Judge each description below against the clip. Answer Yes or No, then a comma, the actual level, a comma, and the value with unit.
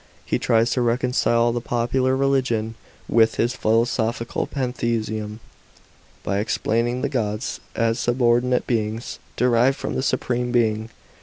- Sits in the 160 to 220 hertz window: No, low, 120 Hz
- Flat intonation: Yes, narrow, 1.8 semitones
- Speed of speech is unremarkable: No, slow, 125 wpm